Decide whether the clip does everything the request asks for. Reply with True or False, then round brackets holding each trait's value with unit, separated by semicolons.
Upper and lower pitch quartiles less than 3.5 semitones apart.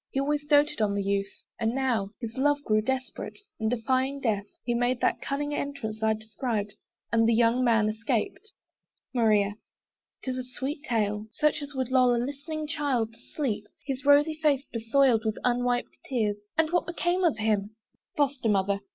False (4.4 semitones)